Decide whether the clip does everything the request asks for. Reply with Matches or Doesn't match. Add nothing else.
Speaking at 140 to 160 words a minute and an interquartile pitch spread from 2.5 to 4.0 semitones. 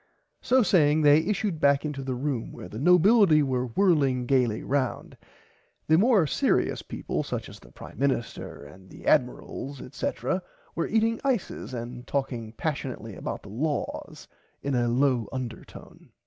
Doesn't match